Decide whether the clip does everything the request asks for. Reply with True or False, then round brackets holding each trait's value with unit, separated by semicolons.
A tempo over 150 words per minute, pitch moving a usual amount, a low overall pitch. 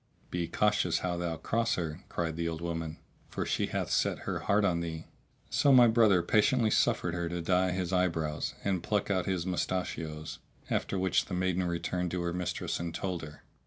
False (195 wpm; 2.1 semitones; 90 Hz)